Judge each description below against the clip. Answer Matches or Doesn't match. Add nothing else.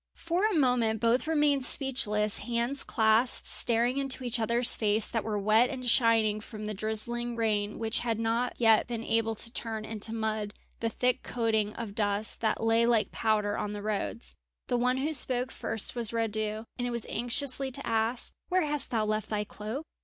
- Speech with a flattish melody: Matches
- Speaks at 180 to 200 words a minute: Matches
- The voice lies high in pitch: Matches